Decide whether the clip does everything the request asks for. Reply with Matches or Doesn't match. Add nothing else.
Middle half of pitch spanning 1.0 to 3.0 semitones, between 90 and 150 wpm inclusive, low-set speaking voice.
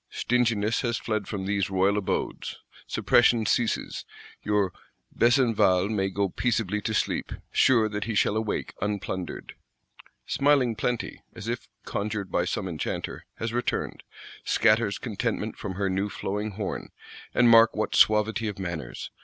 Matches